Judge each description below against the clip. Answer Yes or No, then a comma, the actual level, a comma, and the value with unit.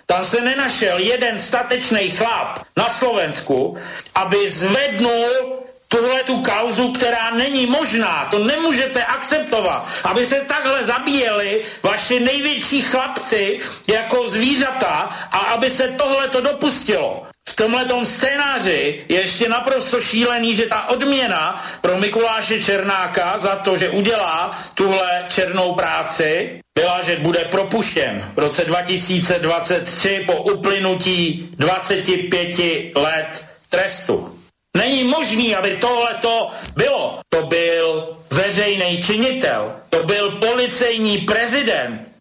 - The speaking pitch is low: No, high, 220 Hz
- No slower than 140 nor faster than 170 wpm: No, slow, 110 wpm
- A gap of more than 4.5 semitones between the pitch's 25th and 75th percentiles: Yes, average, 5.2 semitones